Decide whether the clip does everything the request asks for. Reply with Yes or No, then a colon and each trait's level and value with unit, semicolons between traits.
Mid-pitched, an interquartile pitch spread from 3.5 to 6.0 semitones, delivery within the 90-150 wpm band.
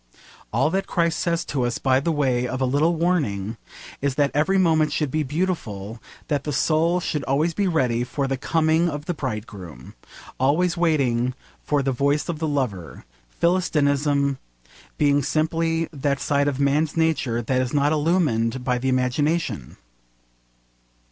No: medium, 145 Hz; average, 3.9 semitones; average, 160 wpm